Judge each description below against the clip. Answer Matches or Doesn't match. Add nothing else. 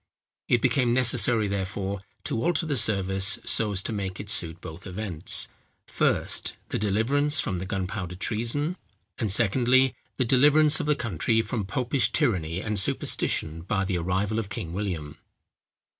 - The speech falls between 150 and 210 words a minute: Matches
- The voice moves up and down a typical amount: Matches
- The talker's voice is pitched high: Doesn't match